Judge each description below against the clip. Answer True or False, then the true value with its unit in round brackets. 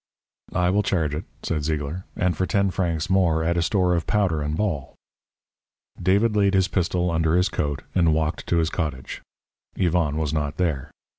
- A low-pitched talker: True (85 Hz)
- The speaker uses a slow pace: False (180 wpm)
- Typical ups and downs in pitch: True (3.1 semitones)